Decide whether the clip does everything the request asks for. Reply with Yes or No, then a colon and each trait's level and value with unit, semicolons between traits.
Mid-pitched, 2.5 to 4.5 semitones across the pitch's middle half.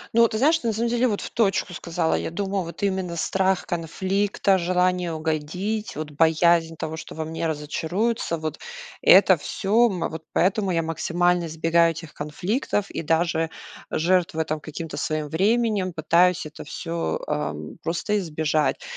Yes: medium, 170 Hz; average, 3.3 semitones